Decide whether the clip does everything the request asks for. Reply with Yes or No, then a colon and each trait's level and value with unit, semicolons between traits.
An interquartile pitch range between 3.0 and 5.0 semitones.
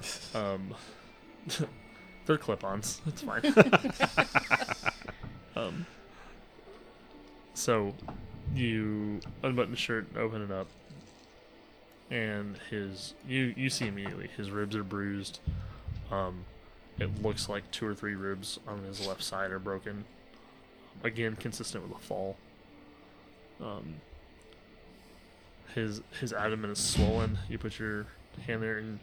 No: narrow, 2.4 semitones